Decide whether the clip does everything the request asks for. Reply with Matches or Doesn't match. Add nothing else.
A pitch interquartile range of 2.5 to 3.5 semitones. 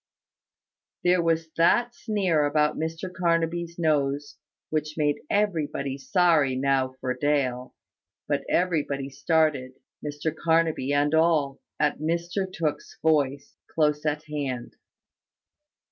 Matches